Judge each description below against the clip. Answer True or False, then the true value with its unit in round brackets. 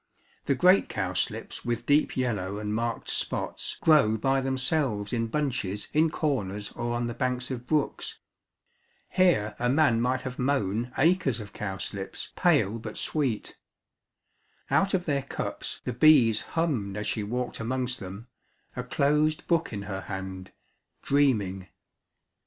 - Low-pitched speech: True (125 Hz)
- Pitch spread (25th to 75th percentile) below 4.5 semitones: False (5.3 semitones)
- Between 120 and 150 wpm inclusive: True (140 wpm)